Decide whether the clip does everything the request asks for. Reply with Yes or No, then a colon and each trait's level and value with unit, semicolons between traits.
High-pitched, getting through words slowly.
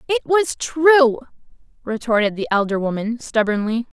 Yes: high, 245 Hz; slow, 120 wpm